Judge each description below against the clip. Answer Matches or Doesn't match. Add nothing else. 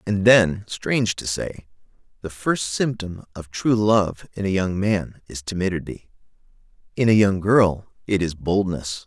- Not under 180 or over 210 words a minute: Doesn't match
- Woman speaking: Doesn't match